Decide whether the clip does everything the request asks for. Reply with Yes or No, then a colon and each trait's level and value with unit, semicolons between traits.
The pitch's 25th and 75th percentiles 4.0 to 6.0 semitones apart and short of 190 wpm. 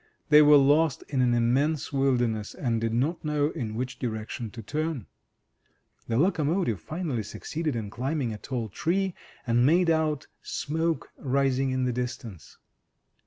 Yes: average, 4.6 semitones; average, 150 wpm